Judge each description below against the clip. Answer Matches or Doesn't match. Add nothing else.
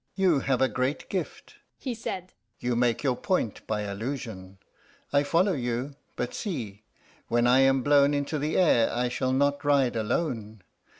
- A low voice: Matches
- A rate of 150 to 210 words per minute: Matches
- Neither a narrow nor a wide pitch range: Matches